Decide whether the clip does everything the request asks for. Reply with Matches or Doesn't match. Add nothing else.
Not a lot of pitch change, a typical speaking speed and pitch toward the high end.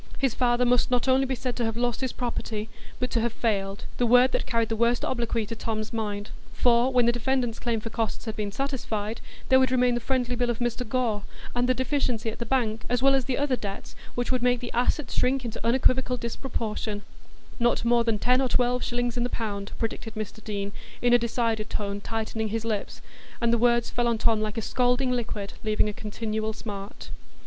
Doesn't match